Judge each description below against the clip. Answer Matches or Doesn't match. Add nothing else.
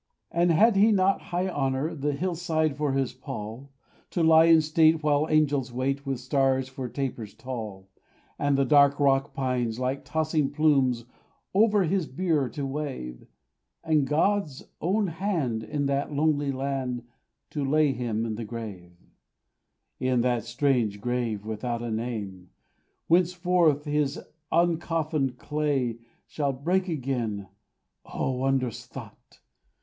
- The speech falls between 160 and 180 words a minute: Doesn't match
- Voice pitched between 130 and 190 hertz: Matches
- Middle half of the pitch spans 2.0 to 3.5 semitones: Doesn't match